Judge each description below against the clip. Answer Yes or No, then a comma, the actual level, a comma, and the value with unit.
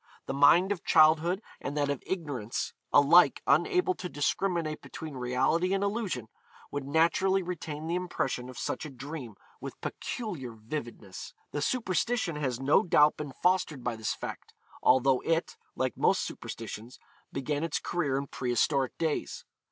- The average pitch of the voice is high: No, medium, 150 Hz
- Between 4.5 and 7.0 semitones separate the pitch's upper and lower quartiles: Yes, average, 5.1 semitones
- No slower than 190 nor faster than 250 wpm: No, average, 150 wpm